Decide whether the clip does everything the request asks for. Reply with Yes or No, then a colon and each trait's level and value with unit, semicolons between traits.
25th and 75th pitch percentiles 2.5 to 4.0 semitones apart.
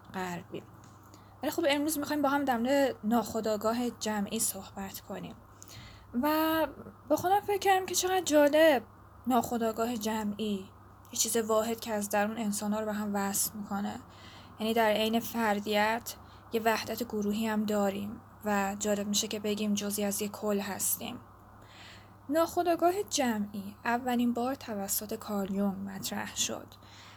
Yes: average, 3.2 semitones